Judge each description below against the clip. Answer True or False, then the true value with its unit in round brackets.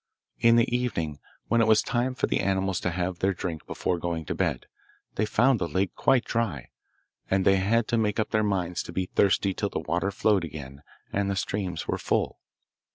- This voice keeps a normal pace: False (210 wpm)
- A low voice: True (95 Hz)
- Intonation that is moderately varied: True (3.8 semitones)